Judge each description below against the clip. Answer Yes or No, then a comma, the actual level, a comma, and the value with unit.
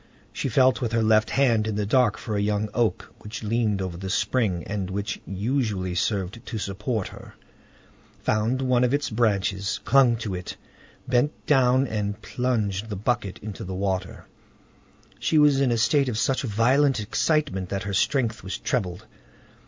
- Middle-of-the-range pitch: No, low, 110 Hz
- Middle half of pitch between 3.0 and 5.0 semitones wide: Yes, average, 4.1 semitones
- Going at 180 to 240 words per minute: No, average, 170 wpm